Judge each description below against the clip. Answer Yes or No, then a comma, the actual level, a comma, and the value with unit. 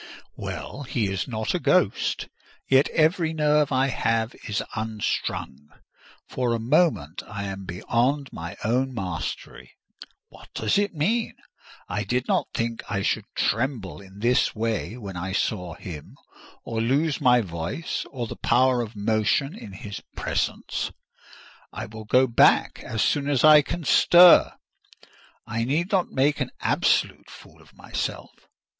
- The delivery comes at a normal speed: Yes, average, 150 wpm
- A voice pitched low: Yes, low, 115 Hz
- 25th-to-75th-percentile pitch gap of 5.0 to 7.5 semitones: Yes, average, 5.3 semitones